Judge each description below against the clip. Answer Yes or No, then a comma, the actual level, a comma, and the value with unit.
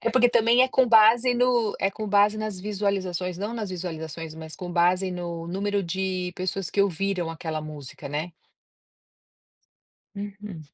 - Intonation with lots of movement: No, average, 3.6 semitones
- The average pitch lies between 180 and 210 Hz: Yes, high, 190 Hz